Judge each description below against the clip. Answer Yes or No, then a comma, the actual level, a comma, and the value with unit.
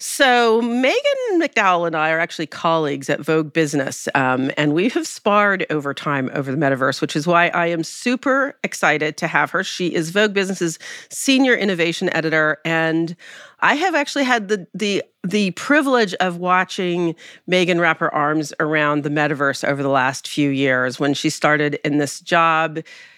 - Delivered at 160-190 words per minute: Yes, average, 175 wpm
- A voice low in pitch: No, medium, 165 Hz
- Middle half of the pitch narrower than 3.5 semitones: No, average, 4.8 semitones